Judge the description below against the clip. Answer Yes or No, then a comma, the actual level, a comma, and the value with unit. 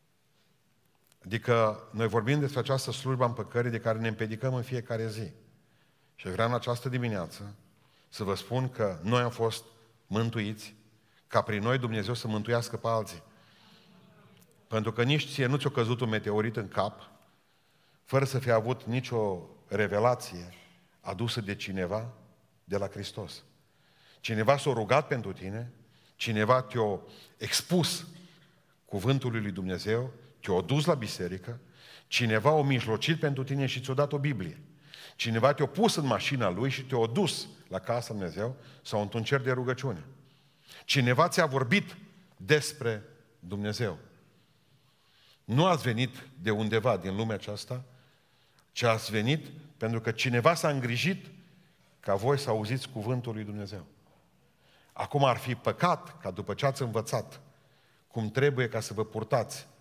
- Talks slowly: No, average, 145 wpm